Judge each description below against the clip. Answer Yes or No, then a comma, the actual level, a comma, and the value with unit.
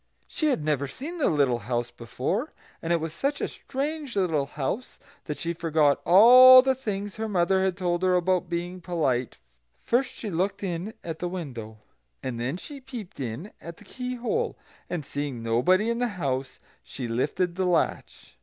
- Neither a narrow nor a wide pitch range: No, wide, 7.4 semitones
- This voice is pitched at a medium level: Yes, medium, 175 Hz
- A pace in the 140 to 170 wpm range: No, average, 180 wpm